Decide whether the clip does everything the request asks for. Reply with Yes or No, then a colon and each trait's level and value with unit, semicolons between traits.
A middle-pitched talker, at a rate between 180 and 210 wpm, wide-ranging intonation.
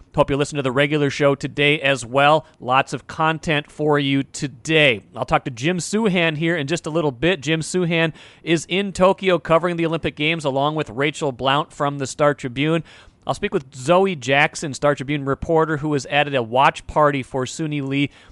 No: medium, 150 Hz; average, 200 wpm; narrow, 2.6 semitones